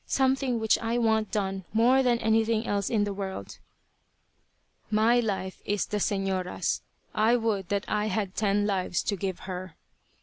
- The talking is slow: No, average, 160 wpm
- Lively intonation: No, narrow, 2.6 semitones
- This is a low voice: No, high, 210 Hz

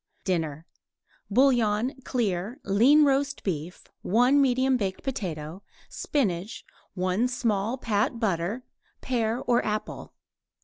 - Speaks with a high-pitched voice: Yes, high, 220 Hz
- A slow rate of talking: Yes, slow, 100 wpm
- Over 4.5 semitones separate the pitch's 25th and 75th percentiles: Yes, average, 5.3 semitones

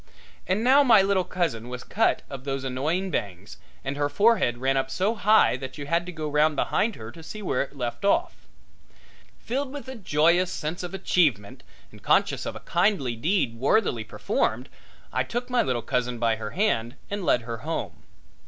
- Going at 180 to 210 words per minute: Yes, average, 190 wpm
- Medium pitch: Yes, medium, 155 Hz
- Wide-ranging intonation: Yes, wide, 8.0 semitones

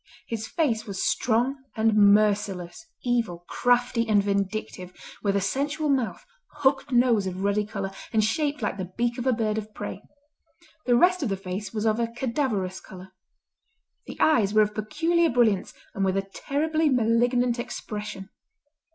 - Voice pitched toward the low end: No, high, 220 Hz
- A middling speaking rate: Yes, average, 160 wpm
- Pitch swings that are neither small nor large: Yes, average, 3.8 semitones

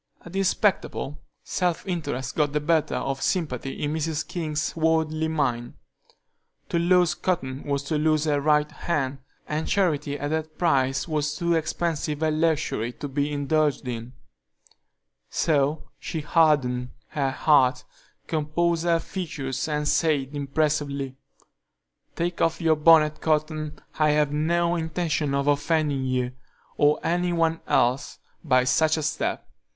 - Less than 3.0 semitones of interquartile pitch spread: Yes, narrow, 2.4 semitones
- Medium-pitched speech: Yes, medium, 150 Hz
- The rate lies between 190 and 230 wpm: No, average, 140 wpm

